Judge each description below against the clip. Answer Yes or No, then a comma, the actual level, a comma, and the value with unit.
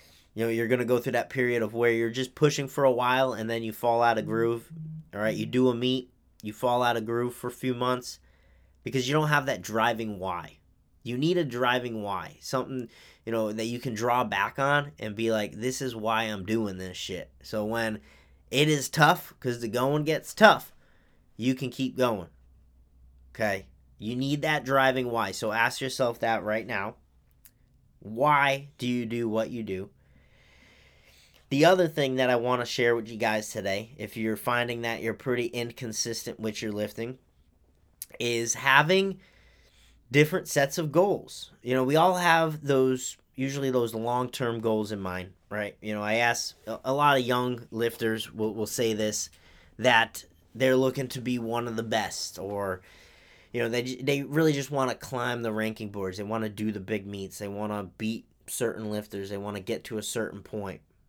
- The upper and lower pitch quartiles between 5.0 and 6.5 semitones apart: No, average, 3.5 semitones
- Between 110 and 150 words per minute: No, average, 195 wpm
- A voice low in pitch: Yes, low, 115 Hz